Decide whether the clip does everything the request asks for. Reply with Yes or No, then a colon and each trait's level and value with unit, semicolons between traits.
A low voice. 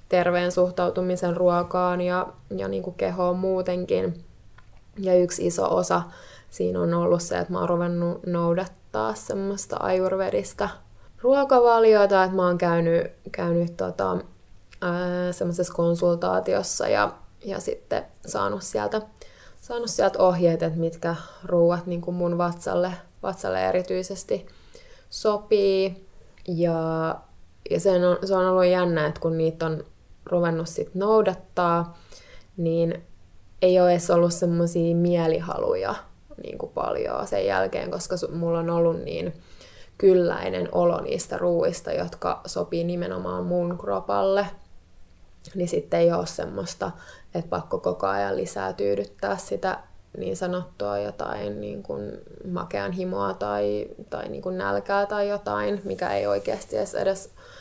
No: medium, 170 Hz